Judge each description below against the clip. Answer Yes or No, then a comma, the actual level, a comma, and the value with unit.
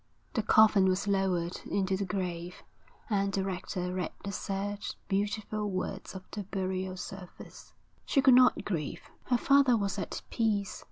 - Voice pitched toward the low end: No, high, 195 Hz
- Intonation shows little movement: Yes, narrow, 2.0 semitones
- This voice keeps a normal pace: Yes, average, 155 wpm